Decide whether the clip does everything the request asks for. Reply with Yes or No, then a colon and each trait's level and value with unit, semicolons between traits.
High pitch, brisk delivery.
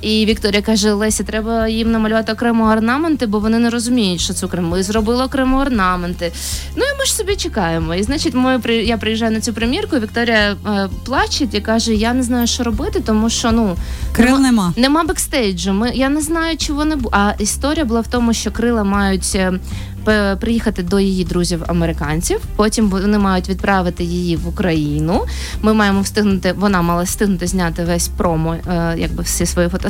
Yes: high, 215 Hz; fast, 185 wpm